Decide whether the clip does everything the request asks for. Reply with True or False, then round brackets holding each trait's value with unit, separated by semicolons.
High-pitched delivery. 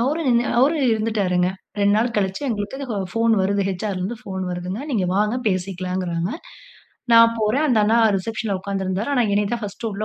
True (210 Hz)